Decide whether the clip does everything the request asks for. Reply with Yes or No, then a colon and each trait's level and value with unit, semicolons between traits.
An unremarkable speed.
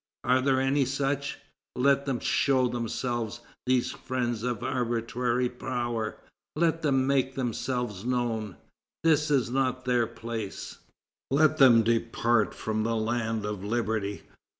No: slow, 125 wpm